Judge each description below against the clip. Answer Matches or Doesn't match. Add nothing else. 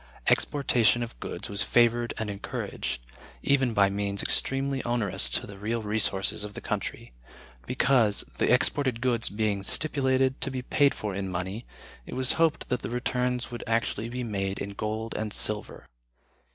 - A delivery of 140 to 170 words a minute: Matches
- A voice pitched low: Matches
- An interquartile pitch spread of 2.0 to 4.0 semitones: Matches